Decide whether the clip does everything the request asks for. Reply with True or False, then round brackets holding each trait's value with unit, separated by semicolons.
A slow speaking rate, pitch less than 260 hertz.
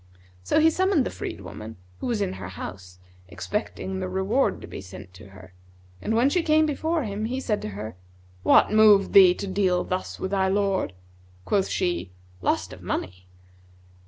False (185 wpm; 190 Hz)